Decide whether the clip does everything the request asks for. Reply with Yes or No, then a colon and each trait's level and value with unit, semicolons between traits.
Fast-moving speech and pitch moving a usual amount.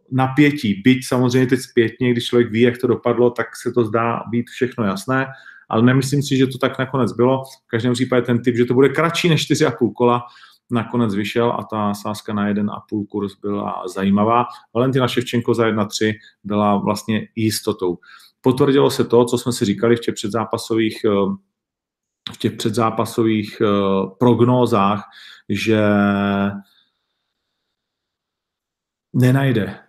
No: average, 145 wpm; average, 3.0 semitones